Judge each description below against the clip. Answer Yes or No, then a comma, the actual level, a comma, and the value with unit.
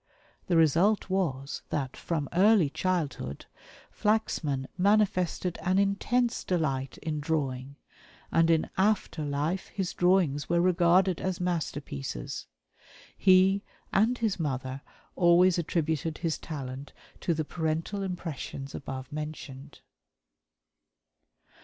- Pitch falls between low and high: Yes, medium, 165 Hz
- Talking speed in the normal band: No, slow, 105 wpm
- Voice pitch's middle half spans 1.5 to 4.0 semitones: No, average, 4.5 semitones